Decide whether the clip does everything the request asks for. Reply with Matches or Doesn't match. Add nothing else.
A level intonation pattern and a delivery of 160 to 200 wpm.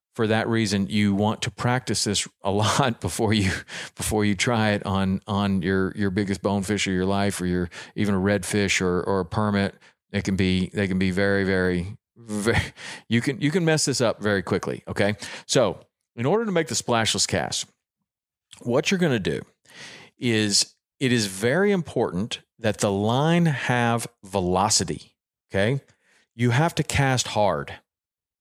Doesn't match